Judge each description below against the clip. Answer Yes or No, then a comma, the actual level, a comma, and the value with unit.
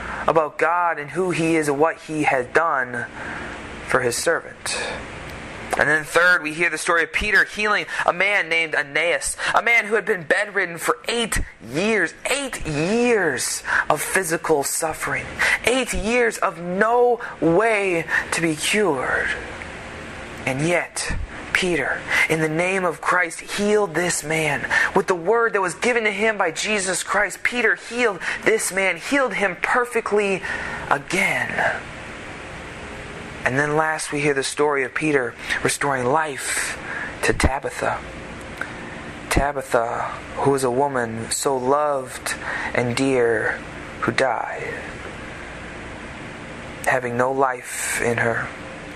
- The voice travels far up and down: Yes, wide, 6.5 semitones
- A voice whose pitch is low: No, medium, 165 Hz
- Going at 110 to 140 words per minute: Yes, slow, 135 wpm